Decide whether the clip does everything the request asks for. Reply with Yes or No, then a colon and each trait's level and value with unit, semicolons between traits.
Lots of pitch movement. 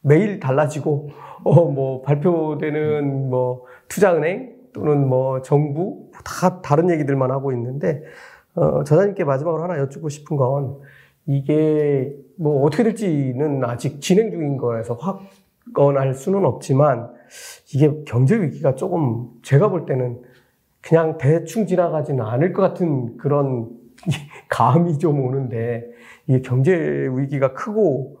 No: average, 3.9 semitones